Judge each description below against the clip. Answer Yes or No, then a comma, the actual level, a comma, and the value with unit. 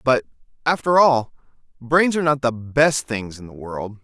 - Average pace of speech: Yes, average, 180 wpm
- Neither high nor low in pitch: No, low, 130 Hz